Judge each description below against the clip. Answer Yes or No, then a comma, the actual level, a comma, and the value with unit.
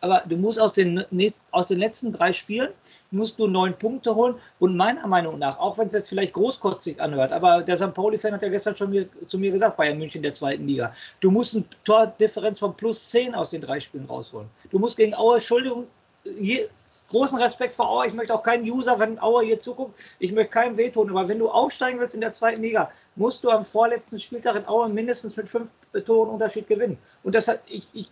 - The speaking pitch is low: No, high, 220 Hz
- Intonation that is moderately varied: Yes, average, 3.2 semitones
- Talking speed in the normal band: No, fast, 230 wpm